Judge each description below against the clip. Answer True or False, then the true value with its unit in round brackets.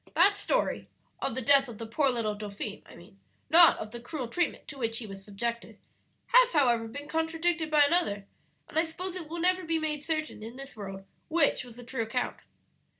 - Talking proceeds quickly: True (210 wpm)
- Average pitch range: False (6.2 semitones)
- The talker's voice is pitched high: True (275 Hz)